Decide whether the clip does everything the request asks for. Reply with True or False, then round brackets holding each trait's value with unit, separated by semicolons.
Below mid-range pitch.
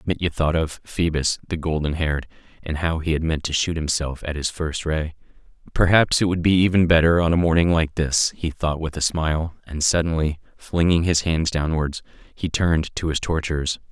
True (80 Hz)